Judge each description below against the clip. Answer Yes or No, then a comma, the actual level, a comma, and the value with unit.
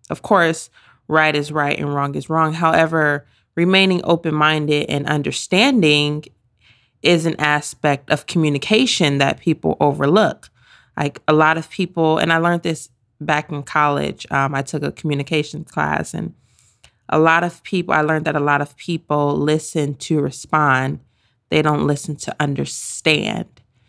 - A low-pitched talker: No, medium, 150 Hz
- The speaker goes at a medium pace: Yes, average, 155 wpm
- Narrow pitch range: Yes, narrow, 2.2 semitones